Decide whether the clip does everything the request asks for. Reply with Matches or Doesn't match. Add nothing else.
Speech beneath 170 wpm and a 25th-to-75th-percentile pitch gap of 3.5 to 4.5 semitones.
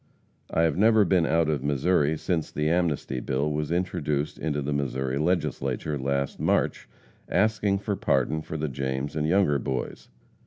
Matches